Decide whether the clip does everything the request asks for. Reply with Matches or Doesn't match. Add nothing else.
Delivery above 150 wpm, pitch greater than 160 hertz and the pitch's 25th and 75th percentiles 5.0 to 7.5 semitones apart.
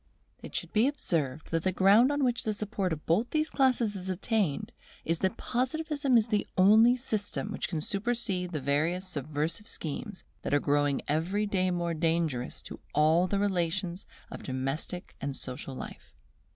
Matches